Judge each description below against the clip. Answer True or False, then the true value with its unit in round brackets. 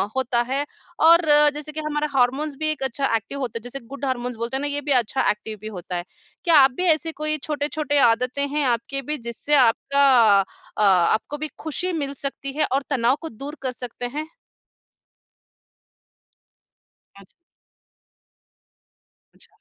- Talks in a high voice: True (275 Hz)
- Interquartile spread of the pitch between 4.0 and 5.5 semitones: False (3.6 semitones)